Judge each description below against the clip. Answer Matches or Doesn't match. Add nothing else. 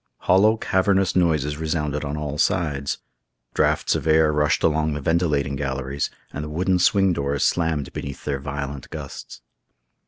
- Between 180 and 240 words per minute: Doesn't match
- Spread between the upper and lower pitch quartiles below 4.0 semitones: Matches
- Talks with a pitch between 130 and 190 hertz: Doesn't match